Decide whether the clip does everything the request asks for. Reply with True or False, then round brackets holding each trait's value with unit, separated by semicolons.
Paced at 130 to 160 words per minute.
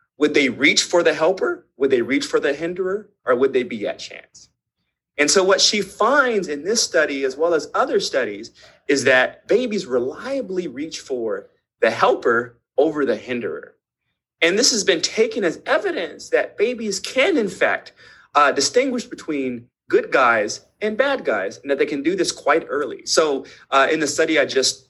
False (185 wpm)